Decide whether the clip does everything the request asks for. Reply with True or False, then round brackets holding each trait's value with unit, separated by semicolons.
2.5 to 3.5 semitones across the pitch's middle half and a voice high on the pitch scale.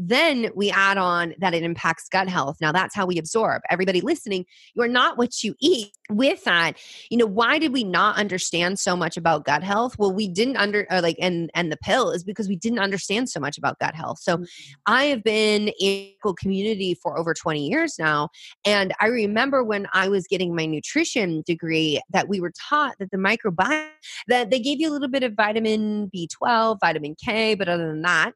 False (4.7 semitones; 200 Hz)